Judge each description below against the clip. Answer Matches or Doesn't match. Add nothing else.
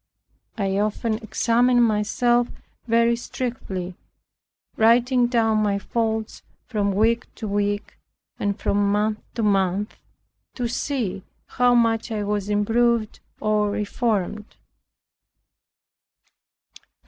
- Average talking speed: Doesn't match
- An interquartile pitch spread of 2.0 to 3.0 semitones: Matches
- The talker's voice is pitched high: Matches